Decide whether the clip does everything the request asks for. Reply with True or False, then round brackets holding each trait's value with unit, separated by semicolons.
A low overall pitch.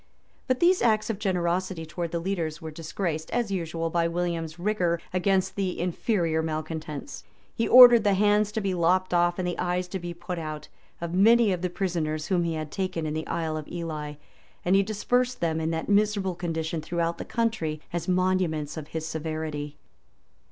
False (175 Hz)